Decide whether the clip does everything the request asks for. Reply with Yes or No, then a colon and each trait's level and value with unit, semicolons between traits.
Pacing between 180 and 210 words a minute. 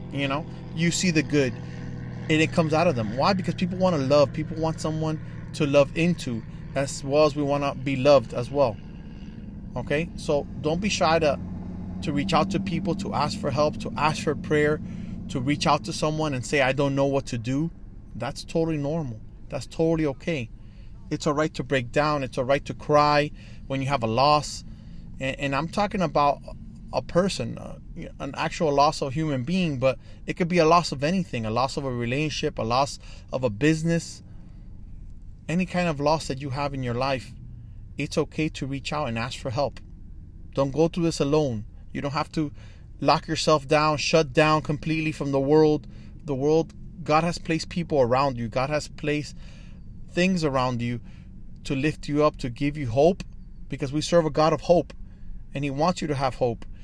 Yes: fast, 205 wpm